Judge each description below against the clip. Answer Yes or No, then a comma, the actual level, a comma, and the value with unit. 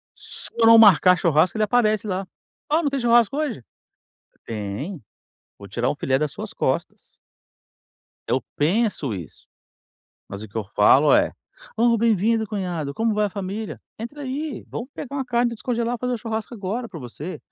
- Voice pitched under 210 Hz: No, high, 215 Hz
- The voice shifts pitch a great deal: Yes, wide, 7.5 semitones